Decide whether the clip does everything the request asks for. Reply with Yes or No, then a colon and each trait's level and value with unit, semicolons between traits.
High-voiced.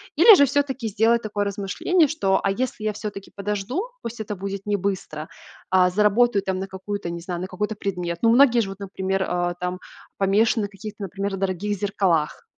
Yes: high, 200 Hz